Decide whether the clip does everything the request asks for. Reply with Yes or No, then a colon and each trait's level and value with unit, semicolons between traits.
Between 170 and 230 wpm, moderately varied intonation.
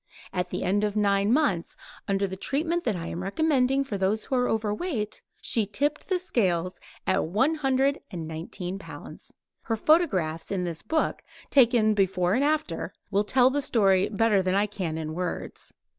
No: average, 175 wpm; wide, 6.3 semitones